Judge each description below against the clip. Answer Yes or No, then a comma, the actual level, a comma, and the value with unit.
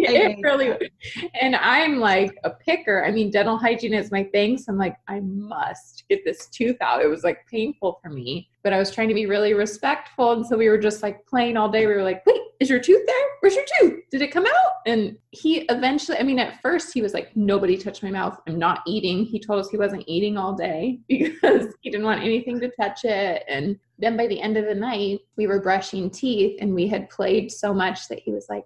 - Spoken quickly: Yes, fast, 245 wpm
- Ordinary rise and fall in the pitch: Yes, average, 4.2 semitones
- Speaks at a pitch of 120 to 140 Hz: No, high, 215 Hz